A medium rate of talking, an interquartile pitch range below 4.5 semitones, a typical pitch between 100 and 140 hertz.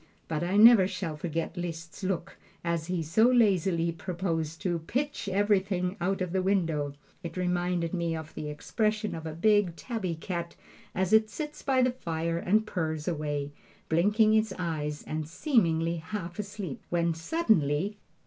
No: average, 160 wpm; average, 4.0 semitones; medium, 175 Hz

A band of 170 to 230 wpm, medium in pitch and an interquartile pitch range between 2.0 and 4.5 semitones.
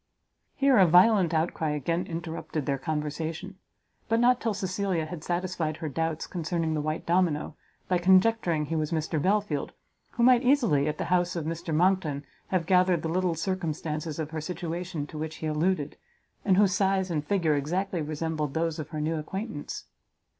Yes: average, 175 wpm; medium, 165 Hz; average, 3.2 semitones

